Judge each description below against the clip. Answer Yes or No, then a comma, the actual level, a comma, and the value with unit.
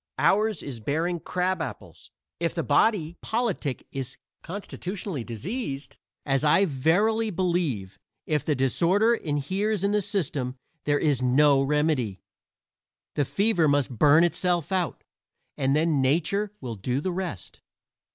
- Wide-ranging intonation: Yes, wide, 5.7 semitones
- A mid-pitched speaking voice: Yes, medium, 155 Hz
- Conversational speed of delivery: No, slow, 130 wpm